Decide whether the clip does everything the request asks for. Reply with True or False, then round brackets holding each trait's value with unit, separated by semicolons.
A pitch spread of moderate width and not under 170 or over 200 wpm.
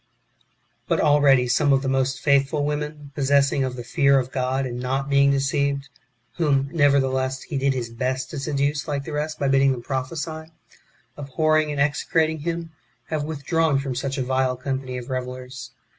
False (2.0 semitones; 185 wpm)